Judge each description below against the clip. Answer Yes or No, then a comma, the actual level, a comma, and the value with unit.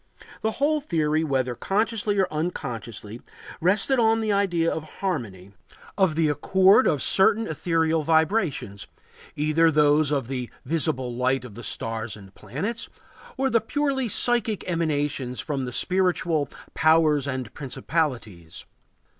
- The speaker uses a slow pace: Yes, slow, 130 wpm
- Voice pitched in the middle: Yes, medium, 155 Hz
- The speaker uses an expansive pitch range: Yes, wide, 6.9 semitones